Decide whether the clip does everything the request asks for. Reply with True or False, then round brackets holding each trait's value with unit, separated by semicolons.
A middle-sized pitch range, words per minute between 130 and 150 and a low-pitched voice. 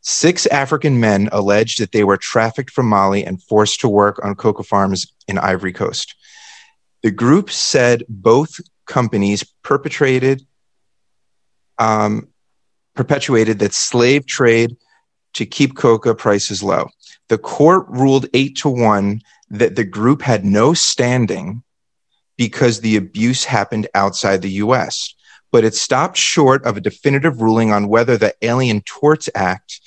True (4.2 semitones; 140 wpm; 115 Hz)